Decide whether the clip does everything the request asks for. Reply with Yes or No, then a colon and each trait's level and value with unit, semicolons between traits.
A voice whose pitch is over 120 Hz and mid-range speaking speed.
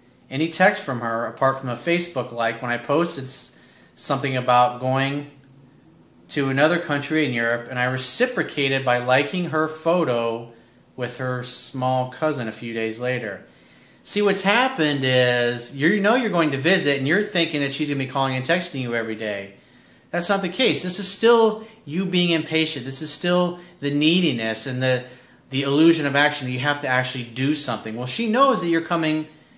Yes: medium, 140 Hz; average, 190 wpm